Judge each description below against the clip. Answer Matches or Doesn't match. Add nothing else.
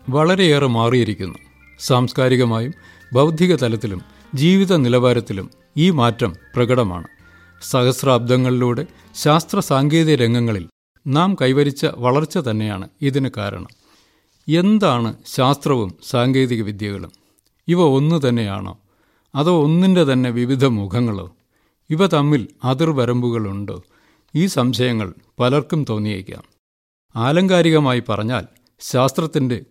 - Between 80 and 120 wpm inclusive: Matches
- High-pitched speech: Doesn't match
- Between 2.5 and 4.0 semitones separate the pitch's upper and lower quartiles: Doesn't match